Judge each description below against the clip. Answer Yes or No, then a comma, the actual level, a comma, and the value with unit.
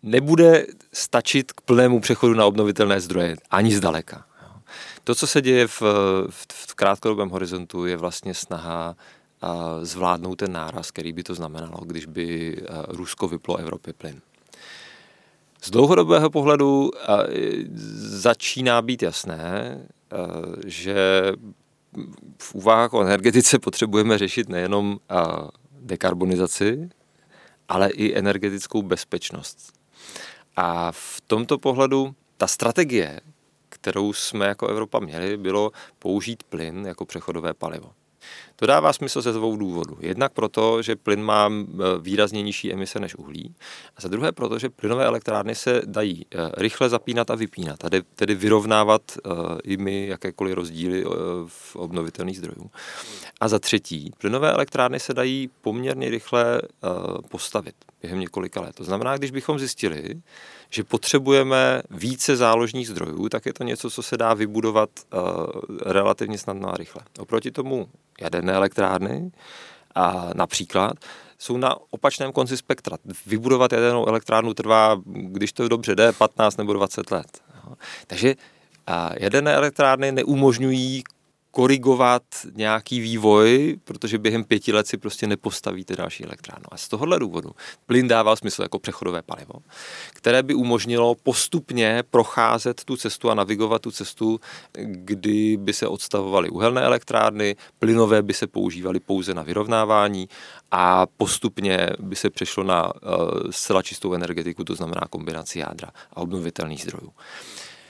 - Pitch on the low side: Yes, low, 105 Hz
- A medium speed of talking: Yes, average, 130 wpm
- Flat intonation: No, average, 4.4 semitones